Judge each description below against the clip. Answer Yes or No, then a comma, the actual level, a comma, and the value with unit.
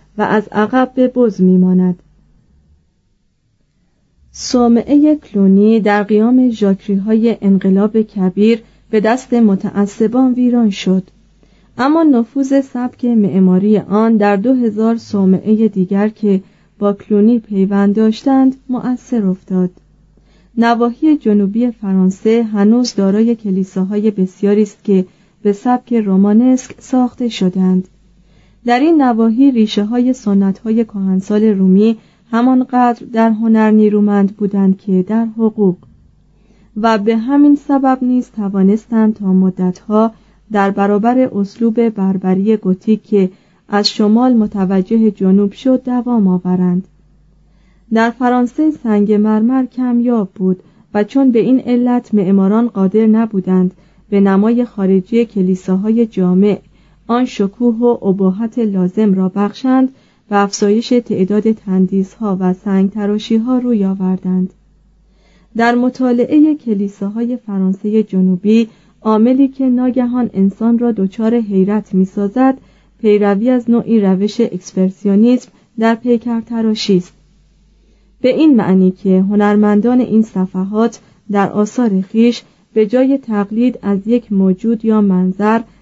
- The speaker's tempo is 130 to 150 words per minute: No, average, 115 wpm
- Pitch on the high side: Yes, high, 210 Hz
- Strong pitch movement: No, average, 3.5 semitones